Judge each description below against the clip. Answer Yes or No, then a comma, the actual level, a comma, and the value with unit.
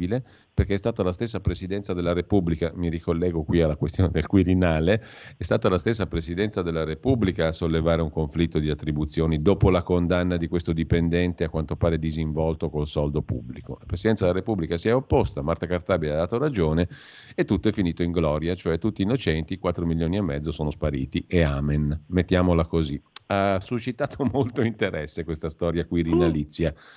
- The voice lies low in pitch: Yes, very low, 85 Hz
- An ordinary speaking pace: No, fast, 175 wpm